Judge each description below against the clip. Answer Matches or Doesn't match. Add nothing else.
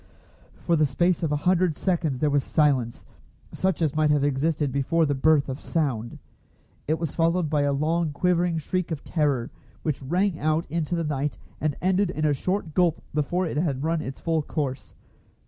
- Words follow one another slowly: Doesn't match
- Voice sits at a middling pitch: Matches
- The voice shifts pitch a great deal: Doesn't match